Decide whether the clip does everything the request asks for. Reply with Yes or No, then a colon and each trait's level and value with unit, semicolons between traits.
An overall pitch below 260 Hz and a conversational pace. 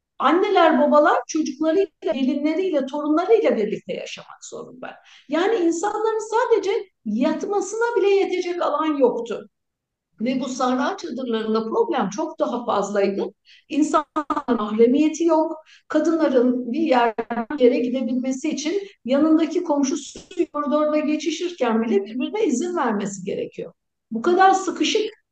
No: very high, 310 Hz; average, 110 wpm